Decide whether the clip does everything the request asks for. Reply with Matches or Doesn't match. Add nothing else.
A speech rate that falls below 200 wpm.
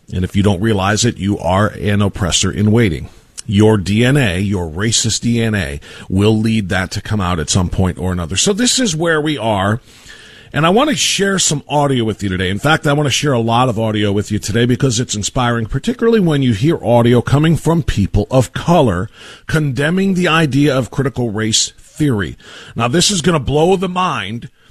Doesn't match